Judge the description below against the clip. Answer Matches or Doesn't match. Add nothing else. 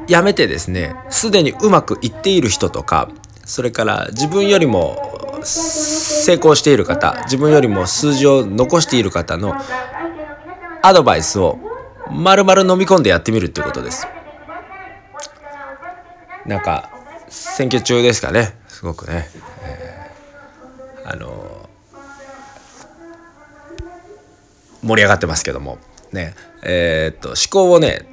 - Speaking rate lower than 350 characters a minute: Matches